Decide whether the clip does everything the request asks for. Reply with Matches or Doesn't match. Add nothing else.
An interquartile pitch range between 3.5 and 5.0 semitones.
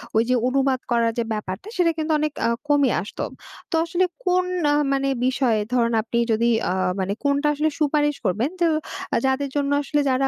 Matches